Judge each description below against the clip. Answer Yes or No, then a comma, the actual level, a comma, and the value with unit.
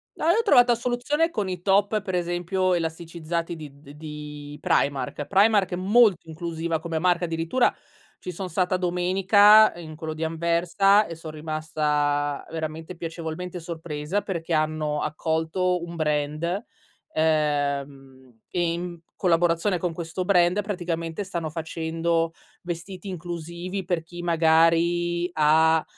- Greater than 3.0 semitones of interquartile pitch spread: No, narrow, 2.5 semitones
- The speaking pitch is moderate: Yes, medium, 170 Hz